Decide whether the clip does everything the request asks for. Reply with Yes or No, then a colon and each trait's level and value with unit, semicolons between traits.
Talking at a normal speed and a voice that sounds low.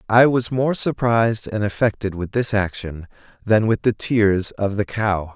Yes: average, 180 wpm; low, 105 Hz